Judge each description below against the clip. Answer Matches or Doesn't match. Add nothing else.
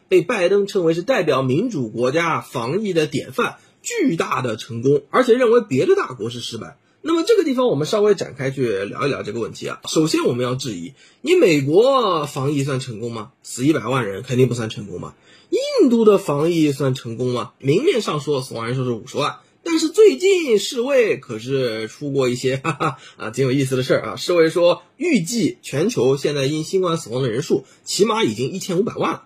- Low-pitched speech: Doesn't match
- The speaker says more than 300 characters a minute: Matches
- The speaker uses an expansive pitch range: Matches